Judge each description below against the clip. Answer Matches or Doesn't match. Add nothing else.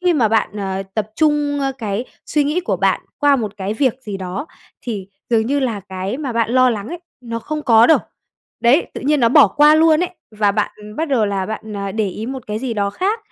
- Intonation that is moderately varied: Doesn't match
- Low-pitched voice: Doesn't match